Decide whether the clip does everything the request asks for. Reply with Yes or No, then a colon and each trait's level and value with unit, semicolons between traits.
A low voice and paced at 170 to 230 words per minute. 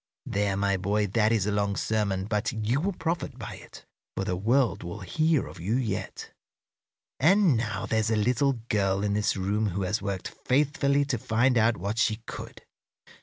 Yes: low, 110 Hz; average, 185 wpm